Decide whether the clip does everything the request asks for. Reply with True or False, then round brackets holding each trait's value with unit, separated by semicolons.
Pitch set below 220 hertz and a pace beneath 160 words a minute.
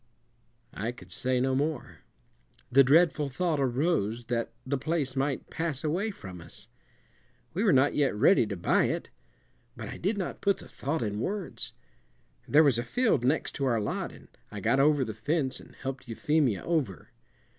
False (135 Hz; 175 wpm)